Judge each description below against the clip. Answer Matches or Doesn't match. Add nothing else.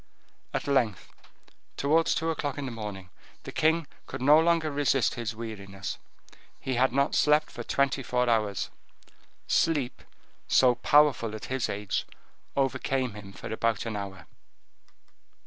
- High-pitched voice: Doesn't match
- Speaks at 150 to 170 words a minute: Doesn't match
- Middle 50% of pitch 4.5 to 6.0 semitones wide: Matches